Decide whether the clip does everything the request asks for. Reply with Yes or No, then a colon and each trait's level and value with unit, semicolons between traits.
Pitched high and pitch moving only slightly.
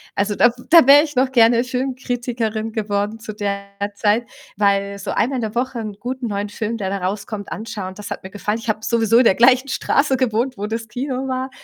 No: high, 225 Hz; average, 3.5 semitones